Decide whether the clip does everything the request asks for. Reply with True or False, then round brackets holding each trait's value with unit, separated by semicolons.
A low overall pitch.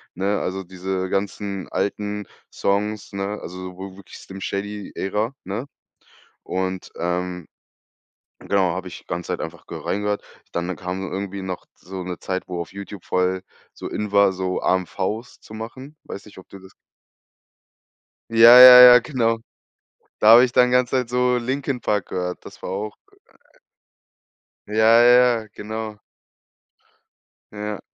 True (100 Hz)